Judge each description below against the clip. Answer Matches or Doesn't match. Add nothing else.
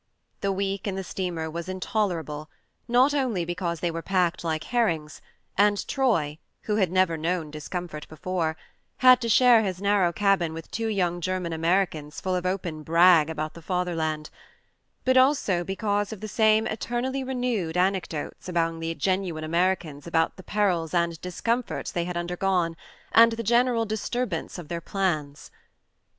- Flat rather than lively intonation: Doesn't match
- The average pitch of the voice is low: Doesn't match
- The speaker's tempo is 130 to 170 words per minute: Matches